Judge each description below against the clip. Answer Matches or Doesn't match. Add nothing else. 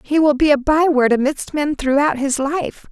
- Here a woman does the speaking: Matches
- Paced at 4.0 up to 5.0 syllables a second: Matches